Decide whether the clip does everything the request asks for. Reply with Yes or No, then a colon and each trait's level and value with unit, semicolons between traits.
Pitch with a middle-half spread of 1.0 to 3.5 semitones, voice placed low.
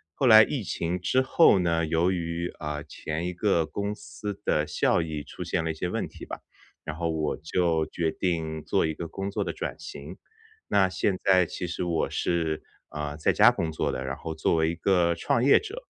Yes: average, 2.7 semitones; very low, 85 Hz